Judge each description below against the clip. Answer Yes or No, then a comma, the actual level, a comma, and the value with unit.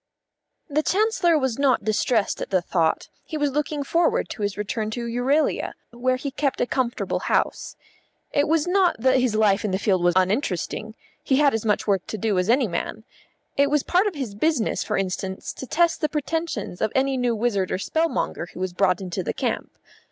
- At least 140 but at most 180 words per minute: No, fast, 205 wpm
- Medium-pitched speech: No, high, 245 Hz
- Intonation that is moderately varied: No, wide, 6.5 semitones